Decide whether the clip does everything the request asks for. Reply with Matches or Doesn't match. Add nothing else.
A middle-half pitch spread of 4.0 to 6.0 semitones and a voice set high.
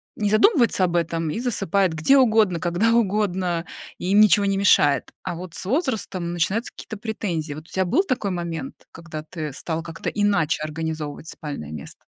Doesn't match